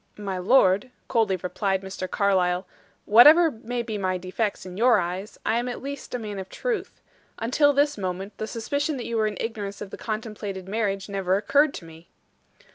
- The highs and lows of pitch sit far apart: No, average, 4.0 semitones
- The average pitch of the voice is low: No, high, 210 Hz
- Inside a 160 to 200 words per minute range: Yes, average, 190 wpm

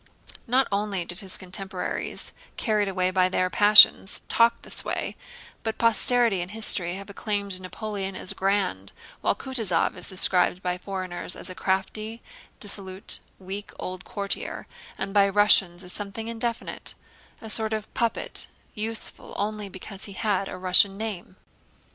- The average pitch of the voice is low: No, high, 200 Hz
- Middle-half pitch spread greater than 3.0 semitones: No, narrow, 2.6 semitones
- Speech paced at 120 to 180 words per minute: Yes, average, 145 wpm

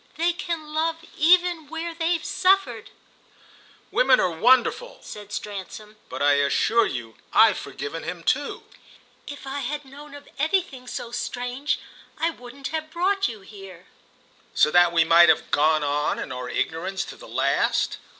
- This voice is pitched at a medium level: No, very high, 255 Hz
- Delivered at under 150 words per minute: No, average, 155 wpm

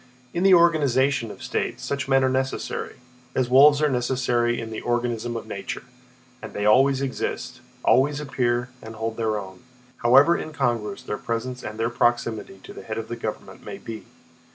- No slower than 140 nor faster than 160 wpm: No, average, 175 wpm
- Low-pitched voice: Yes, low, 120 Hz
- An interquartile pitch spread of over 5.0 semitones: No, average, 3.0 semitones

